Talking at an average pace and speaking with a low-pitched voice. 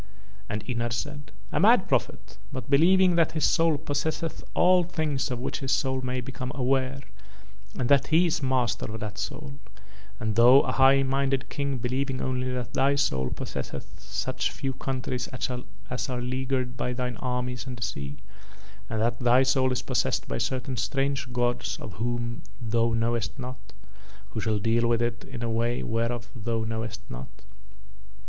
Yes: average, 170 wpm; low, 125 Hz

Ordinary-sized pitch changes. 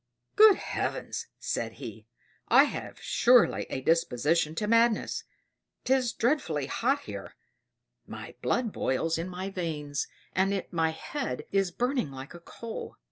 No: wide, 6.9 semitones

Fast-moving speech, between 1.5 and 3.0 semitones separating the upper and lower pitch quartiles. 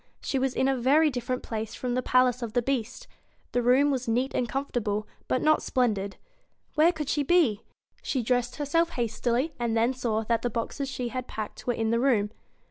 Yes: fast, 230 wpm; average, 2.7 semitones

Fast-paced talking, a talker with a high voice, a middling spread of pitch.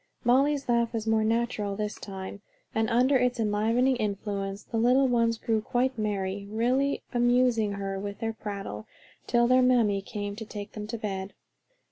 No: average, 165 wpm; high, 225 Hz; average, 3.0 semitones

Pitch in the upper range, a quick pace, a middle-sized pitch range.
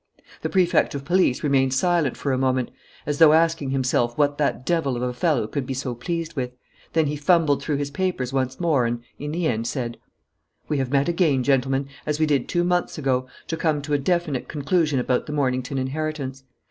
No: medium, 140 Hz; fast, 210 wpm; average, 3.4 semitones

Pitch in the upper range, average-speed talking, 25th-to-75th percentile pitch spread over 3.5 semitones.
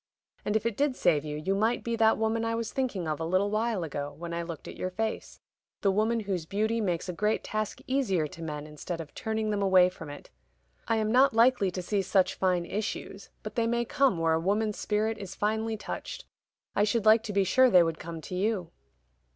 No: high, 205 Hz; fast, 230 wpm; average, 4.3 semitones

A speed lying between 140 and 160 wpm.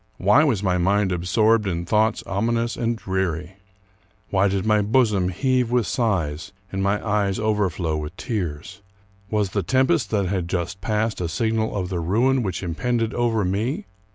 No: average, 170 wpm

